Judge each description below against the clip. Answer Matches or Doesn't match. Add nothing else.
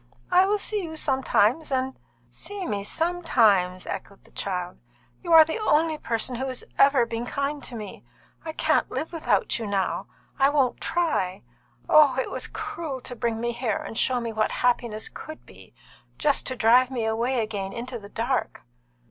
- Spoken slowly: Doesn't match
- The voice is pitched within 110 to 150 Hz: Doesn't match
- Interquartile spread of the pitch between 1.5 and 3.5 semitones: Doesn't match